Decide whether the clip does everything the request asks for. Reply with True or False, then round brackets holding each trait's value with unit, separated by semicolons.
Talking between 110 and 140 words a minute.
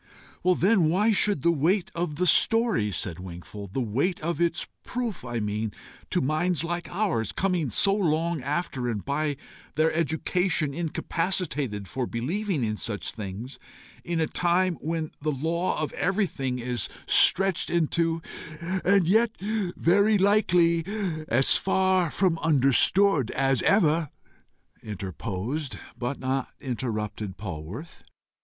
True (135 wpm)